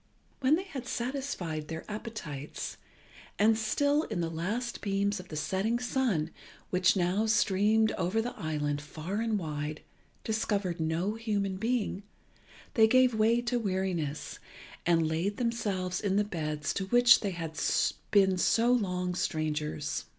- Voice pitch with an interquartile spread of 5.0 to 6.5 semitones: Yes, average, 5.3 semitones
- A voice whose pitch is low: No, high, 195 Hz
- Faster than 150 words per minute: No, average, 145 wpm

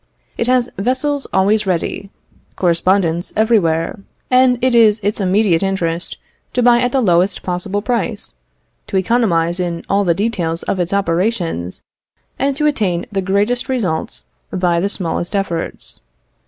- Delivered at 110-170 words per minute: Yes, average, 140 wpm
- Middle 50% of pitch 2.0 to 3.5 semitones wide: No, average, 5.1 semitones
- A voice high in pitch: Yes, high, 195 Hz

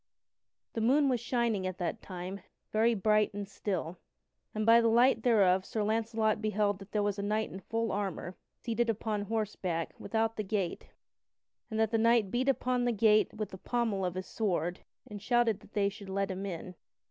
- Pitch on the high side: Yes, high, 215 Hz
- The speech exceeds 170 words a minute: Yes, average, 195 wpm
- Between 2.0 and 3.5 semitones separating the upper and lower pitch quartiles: Yes, average, 2.7 semitones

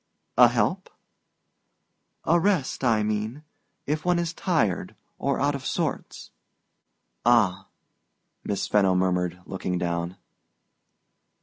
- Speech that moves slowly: Yes, slow, 100 wpm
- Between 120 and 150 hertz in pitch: No, low, 110 Hz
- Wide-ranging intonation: Yes, wide, 8.0 semitones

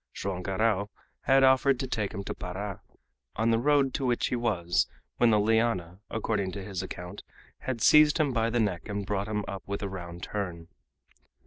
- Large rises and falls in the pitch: No, average, 3.9 semitones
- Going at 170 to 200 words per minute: Yes, average, 195 wpm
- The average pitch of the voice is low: Yes, low, 105 Hz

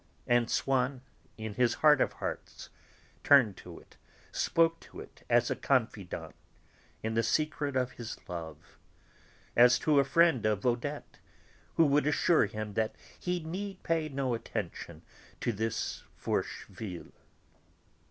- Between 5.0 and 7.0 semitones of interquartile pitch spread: Yes, average, 5.3 semitones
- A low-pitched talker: Yes, low, 125 Hz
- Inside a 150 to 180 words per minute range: No, average, 140 wpm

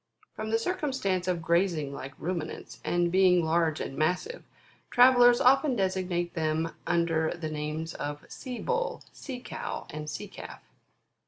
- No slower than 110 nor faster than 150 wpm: Yes, average, 145 wpm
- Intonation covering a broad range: Yes, wide, 7.1 semitones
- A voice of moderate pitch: Yes, medium, 175 Hz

